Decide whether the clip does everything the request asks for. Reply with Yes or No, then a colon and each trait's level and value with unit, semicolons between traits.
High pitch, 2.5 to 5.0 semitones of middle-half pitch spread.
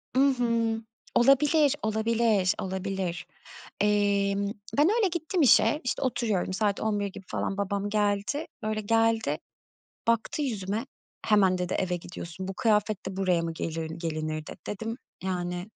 Yes: high, 205 Hz; average, 3.4 semitones